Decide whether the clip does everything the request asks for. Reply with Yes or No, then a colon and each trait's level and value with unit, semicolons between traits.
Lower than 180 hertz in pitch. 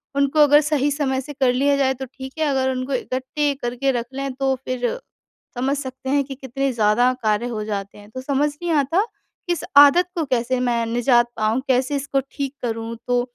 No: very high, 265 Hz